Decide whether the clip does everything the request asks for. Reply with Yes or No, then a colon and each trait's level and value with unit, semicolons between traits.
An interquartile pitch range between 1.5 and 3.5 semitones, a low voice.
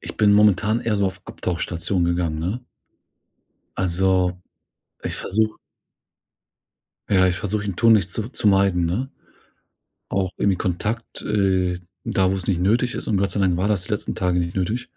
Yes: average, 2.7 semitones; very low, 95 Hz